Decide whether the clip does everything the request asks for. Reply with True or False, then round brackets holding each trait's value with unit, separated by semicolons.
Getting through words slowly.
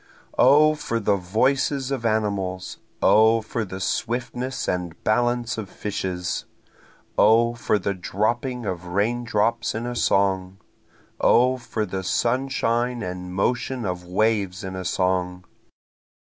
True (125 wpm)